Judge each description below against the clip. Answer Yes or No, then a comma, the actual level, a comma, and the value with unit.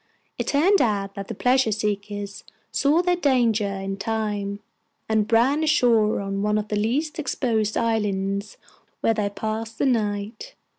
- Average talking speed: Yes, average, 150 wpm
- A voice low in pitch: No, high, 215 Hz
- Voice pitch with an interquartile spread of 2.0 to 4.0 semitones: Yes, average, 3.5 semitones